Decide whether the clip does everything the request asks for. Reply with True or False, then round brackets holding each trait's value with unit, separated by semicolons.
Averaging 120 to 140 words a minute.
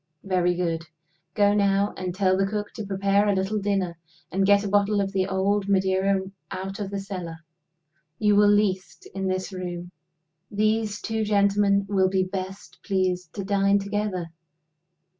False (160 wpm)